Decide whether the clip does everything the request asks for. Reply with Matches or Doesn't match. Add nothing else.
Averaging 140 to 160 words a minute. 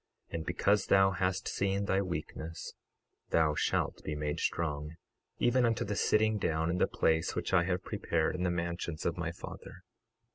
Doesn't match